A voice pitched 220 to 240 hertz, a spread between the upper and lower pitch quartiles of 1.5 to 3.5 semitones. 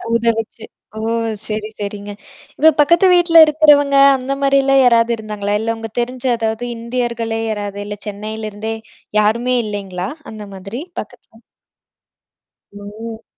Yes: high, 225 Hz; average, 3.2 semitones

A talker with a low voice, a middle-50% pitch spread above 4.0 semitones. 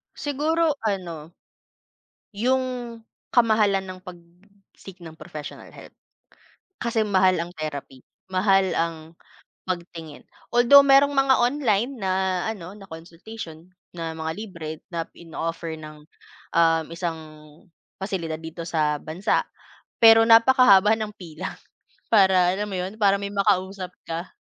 No: high, 190 Hz; average, 4.7 semitones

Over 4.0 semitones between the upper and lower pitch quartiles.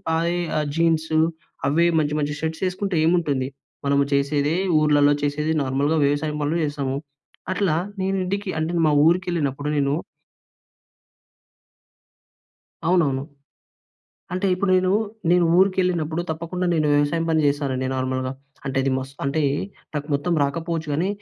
No: average, 3.3 semitones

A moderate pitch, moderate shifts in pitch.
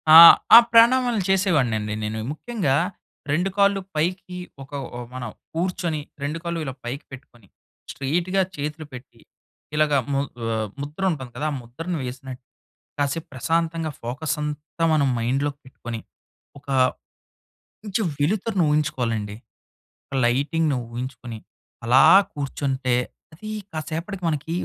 Yes: medium, 150 Hz; average, 4.8 semitones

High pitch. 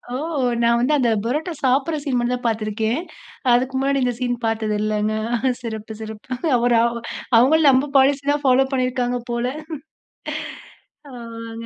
Yes: high, 245 Hz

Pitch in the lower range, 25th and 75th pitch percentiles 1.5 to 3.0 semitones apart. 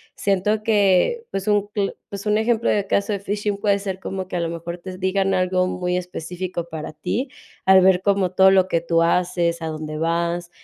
No: medium, 185 Hz; average, 2.7 semitones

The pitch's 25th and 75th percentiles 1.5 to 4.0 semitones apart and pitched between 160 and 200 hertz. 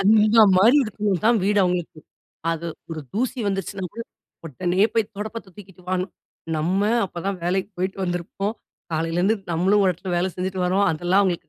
Yes: average, 2.7 semitones; high, 190 Hz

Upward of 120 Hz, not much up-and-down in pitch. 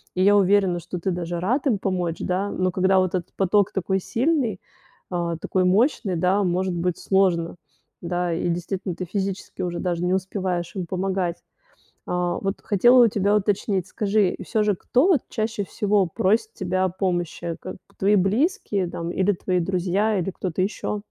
Yes: high, 190 Hz; narrow, 2.3 semitones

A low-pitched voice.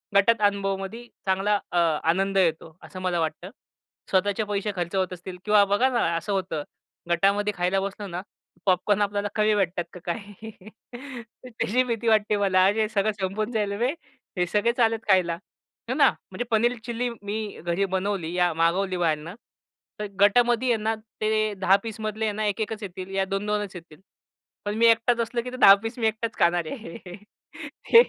No: high, 205 Hz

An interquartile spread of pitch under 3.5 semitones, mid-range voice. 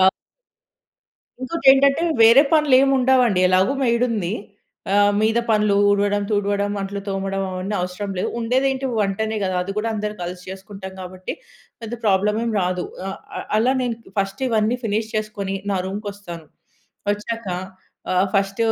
No: average, 2.9 semitones; high, 205 Hz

